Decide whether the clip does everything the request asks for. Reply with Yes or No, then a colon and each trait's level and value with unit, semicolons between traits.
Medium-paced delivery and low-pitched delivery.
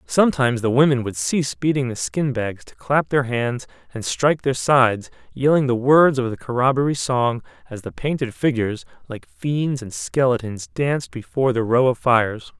Yes: average, 180 wpm; low, 125 Hz